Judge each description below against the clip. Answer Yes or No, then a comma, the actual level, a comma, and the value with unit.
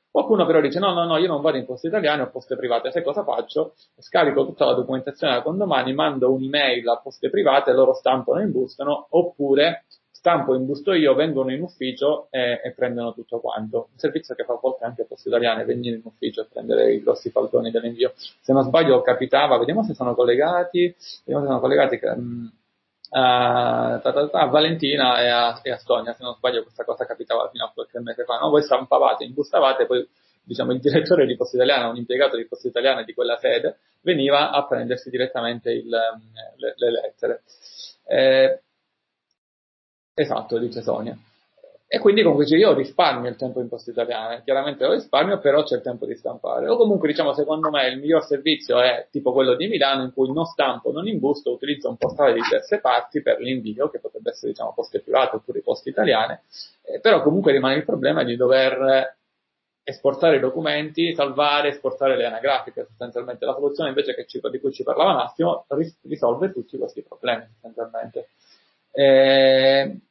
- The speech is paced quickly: Yes, fast, 185 wpm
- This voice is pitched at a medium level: Yes, medium, 145 Hz